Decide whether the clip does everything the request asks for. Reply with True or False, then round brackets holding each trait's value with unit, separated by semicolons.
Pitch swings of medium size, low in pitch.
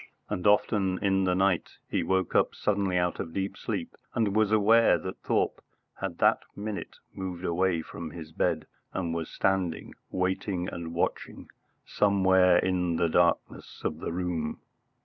False (2.2 semitones; 90 Hz)